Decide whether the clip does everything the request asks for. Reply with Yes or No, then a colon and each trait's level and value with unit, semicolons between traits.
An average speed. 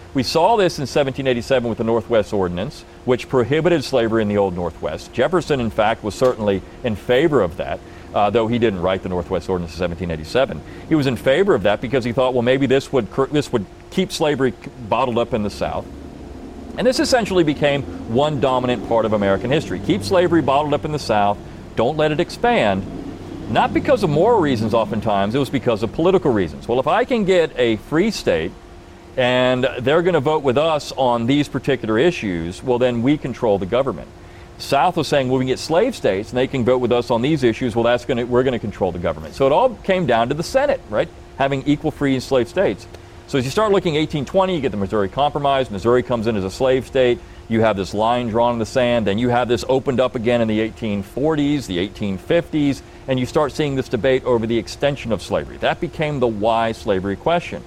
No: fast, 220 wpm